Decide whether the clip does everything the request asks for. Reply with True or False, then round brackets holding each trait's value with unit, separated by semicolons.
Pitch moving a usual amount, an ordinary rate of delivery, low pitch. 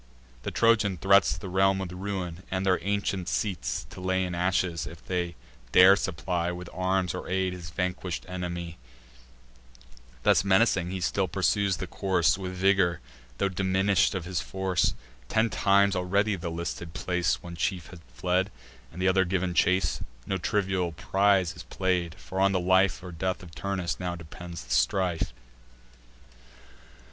False (1.7 semitones; 165 wpm; 95 Hz)